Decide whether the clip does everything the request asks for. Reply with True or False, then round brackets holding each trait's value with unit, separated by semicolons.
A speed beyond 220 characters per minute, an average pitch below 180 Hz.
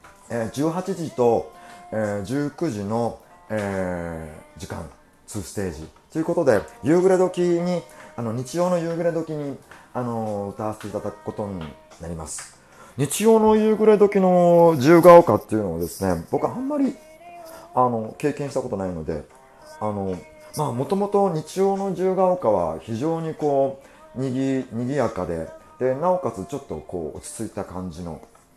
True (295 characters per minute; 135 Hz)